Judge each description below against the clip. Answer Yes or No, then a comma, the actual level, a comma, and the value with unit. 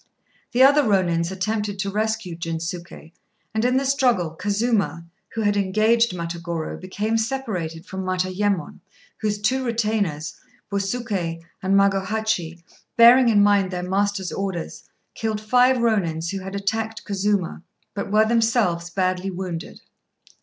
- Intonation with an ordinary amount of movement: Yes, average, 3.6 semitones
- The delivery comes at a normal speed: No, slow, 130 wpm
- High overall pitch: Yes, high, 200 Hz